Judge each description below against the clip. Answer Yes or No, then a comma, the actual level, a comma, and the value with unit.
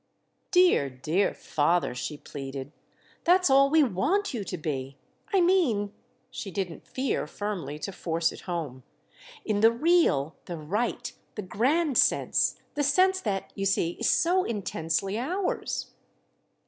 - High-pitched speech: Yes, high, 205 Hz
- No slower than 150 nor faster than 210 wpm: No, slow, 135 wpm